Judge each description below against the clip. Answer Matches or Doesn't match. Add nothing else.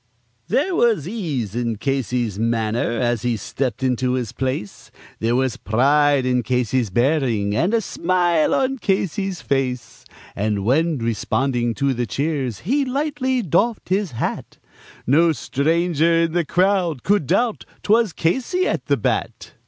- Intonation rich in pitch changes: Matches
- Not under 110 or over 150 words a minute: Matches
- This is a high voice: Doesn't match